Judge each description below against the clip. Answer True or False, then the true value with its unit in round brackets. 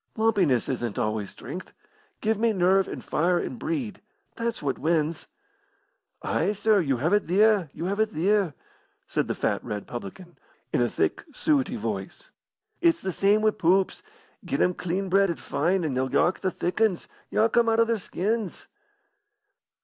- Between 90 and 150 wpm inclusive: False (175 wpm)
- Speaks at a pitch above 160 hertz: True (190 Hz)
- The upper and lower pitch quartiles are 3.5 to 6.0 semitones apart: True (5.1 semitones)